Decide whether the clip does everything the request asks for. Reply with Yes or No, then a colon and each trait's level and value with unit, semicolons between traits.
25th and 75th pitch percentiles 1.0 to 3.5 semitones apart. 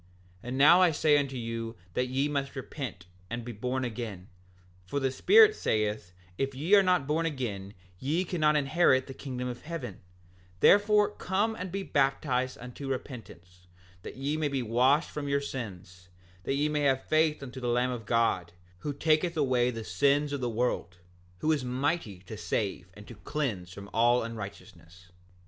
No: average, 4.7 semitones